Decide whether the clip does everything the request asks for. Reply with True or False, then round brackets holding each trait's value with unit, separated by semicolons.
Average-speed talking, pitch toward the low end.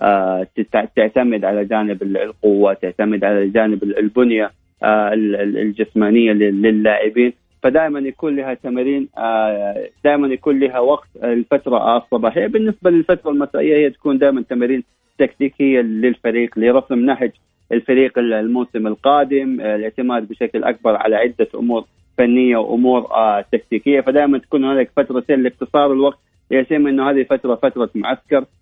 True (115 wpm; 120 Hz)